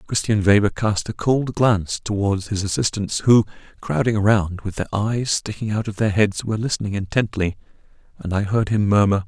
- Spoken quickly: No, average, 180 wpm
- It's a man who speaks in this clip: Yes, male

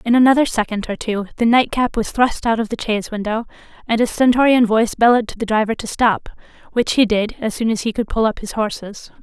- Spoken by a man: No, female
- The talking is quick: Yes, fast, 235 wpm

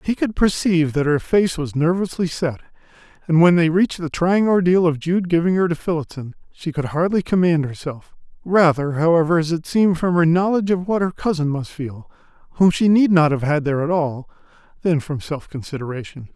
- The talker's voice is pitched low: No, medium, 165 Hz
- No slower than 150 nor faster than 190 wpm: No, average, 200 wpm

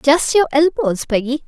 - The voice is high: Yes, very high, 285 Hz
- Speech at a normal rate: Yes, average, 165 wpm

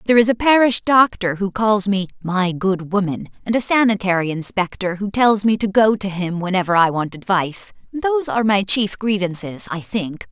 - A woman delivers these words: Yes, female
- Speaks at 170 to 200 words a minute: Yes, average, 190 wpm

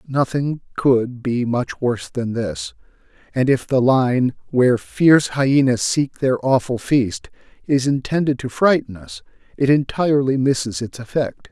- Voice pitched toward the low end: Yes, low, 125 Hz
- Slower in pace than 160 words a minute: Yes, average, 145 wpm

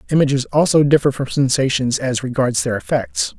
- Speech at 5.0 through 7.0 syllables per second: Yes, 5.4 syllables/s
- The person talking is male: Yes, male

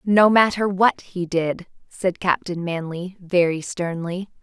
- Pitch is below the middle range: No, medium, 185 Hz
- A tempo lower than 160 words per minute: Yes, slow, 135 wpm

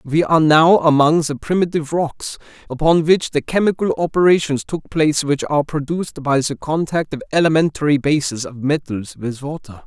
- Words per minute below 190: Yes, average, 165 wpm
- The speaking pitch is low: No, medium, 150 Hz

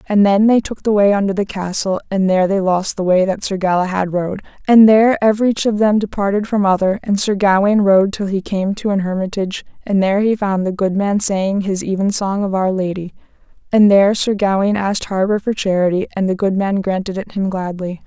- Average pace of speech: No, fast, 220 wpm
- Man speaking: No, female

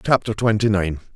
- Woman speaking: No, male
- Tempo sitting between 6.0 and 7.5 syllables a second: No, 5.6 syllables/s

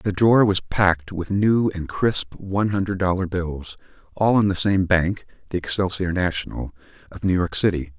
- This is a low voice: Yes, very low, 90 Hz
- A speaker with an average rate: Yes, average, 180 wpm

